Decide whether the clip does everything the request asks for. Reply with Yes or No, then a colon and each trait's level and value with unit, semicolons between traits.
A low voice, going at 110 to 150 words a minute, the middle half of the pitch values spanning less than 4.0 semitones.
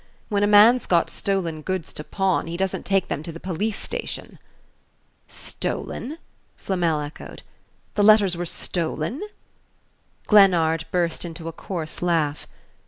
No: medium, 175 Hz; slow, 135 wpm; average, 3.4 semitones